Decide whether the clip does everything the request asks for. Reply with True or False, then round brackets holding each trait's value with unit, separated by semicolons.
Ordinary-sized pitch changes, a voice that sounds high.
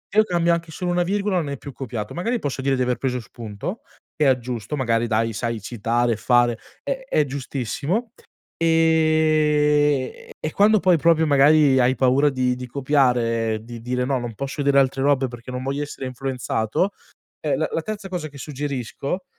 False (4.3 semitones; 135 Hz)